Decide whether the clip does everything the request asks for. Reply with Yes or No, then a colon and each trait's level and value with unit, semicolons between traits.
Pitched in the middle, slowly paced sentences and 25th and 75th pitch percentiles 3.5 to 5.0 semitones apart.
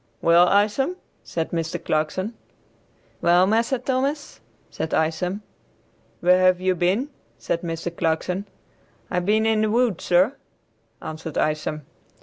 Yes: medium, 180 Hz; slow, 125 wpm; average, 4.6 semitones